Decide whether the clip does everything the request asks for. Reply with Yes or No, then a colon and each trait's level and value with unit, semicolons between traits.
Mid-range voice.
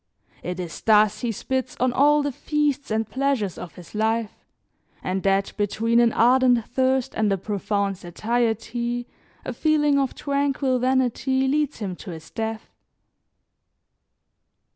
No: high, 235 Hz